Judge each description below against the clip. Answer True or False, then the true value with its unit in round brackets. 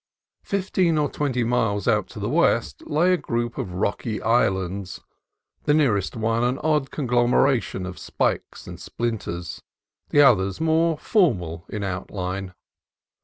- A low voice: True (120 Hz)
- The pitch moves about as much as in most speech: False (7.3 semitones)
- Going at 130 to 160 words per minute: True (140 wpm)